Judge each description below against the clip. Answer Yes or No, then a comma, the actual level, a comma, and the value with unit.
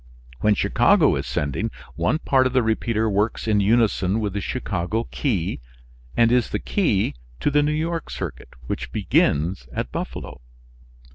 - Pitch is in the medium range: No, low, 110 Hz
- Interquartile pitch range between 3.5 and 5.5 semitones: Yes, average, 4.3 semitones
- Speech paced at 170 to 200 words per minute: No, average, 155 wpm